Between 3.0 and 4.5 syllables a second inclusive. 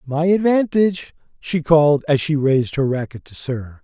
No: 5.3 syllables/s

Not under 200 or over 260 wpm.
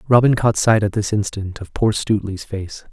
Yes: fast, 205 wpm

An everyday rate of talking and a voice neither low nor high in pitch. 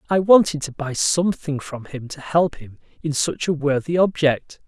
Yes: average, 190 wpm; medium, 150 Hz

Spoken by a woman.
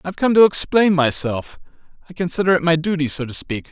No: male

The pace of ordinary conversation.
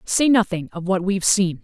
No: fast, 220 wpm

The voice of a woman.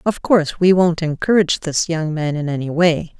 Yes: female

